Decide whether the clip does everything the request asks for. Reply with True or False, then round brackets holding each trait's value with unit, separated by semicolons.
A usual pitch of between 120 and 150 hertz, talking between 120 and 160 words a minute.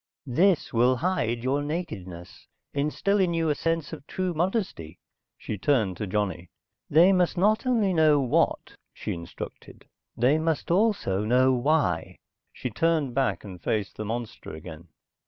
True (140 Hz; 150 wpm)